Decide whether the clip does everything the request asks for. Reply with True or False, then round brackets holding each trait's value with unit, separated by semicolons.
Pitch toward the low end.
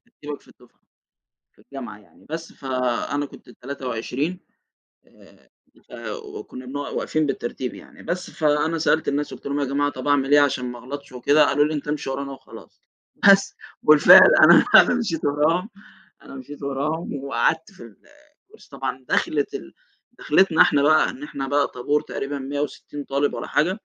False (145 Hz)